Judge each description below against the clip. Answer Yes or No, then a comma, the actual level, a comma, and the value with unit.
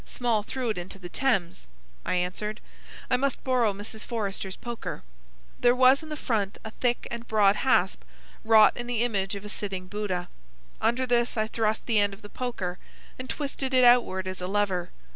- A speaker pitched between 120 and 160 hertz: No, high, 215 Hz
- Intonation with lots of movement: No, average, 3.8 semitones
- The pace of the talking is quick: No, average, 190 wpm